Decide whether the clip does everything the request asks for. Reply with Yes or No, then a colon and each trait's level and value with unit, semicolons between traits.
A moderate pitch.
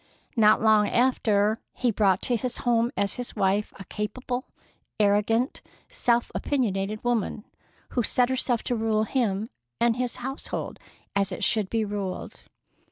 No: high, 225 Hz